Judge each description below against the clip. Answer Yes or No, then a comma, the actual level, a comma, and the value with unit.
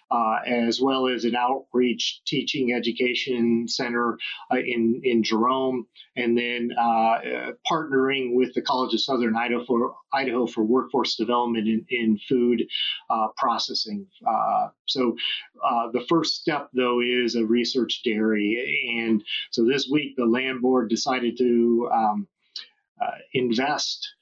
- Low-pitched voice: Yes, low, 120 Hz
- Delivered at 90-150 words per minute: Yes, average, 140 wpm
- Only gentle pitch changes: Yes, narrow, 2.1 semitones